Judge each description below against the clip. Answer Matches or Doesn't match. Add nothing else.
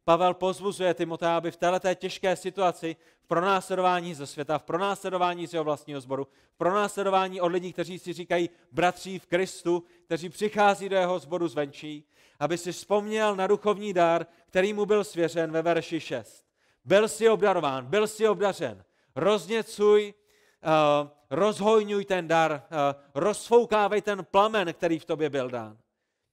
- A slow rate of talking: Doesn't match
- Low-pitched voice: Doesn't match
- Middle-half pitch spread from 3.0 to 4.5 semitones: Matches